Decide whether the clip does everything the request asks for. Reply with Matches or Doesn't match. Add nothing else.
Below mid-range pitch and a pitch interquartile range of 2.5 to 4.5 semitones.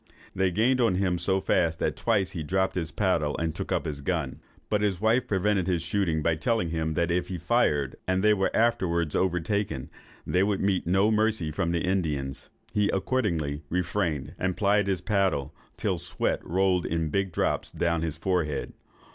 Matches